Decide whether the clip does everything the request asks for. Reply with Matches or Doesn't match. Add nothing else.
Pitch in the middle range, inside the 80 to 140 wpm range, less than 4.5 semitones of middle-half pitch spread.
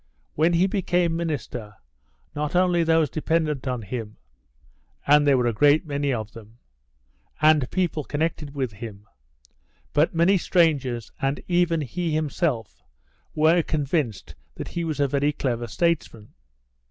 Doesn't match